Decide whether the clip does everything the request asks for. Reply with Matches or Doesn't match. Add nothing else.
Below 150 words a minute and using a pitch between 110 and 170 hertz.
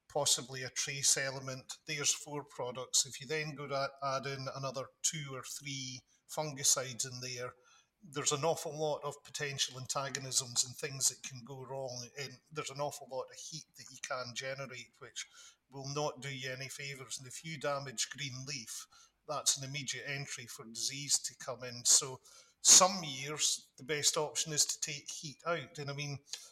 Doesn't match